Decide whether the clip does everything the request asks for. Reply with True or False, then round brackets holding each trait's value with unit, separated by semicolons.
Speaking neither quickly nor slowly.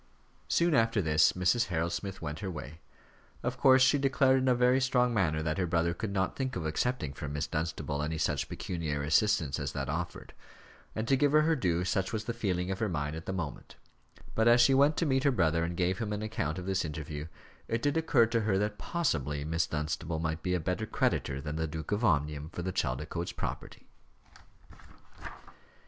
False (210 wpm)